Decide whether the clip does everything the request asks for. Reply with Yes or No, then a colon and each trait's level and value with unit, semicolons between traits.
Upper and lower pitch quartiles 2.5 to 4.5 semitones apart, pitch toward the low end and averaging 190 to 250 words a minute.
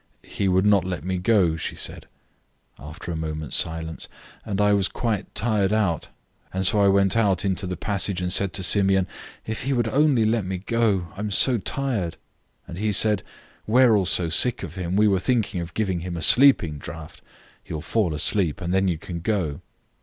Yes: average, 3.8 semitones; very low, 95 Hz; fast, 205 wpm